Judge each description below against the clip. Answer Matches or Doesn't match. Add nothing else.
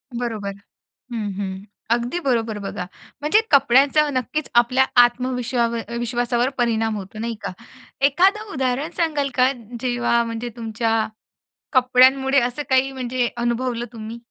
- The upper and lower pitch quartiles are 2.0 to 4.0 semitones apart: Matches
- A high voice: Matches